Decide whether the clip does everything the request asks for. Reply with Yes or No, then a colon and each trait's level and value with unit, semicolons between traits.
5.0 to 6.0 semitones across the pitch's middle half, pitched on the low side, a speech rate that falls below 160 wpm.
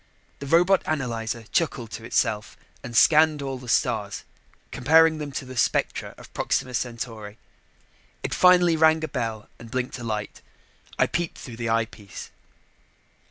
Yes: wide, 5.5 semitones; low, 125 Hz; average, 150 wpm